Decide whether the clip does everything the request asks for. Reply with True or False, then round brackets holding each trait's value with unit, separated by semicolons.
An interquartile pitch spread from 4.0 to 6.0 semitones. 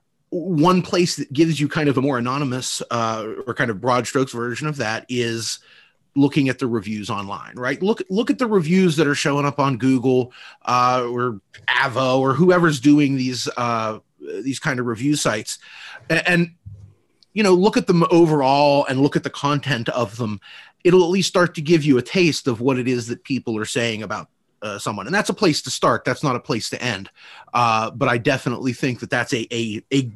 True (4.5 semitones)